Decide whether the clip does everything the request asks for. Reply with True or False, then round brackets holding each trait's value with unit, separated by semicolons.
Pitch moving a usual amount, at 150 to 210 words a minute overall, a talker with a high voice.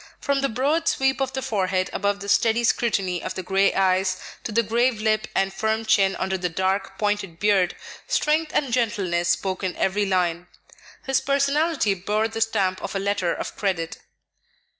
True (3.8 semitones; 180 wpm; 205 Hz)